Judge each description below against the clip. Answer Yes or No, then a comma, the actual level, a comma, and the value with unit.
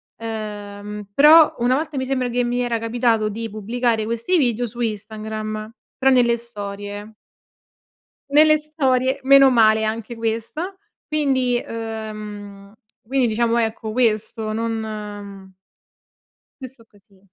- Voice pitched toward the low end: No, high, 230 Hz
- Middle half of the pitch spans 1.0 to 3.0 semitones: Yes, average, 2.7 semitones